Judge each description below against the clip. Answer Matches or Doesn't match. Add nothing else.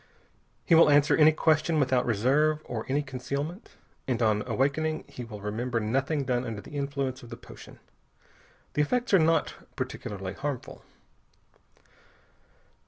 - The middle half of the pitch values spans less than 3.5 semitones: Doesn't match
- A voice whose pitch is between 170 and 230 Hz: Doesn't match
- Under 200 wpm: Matches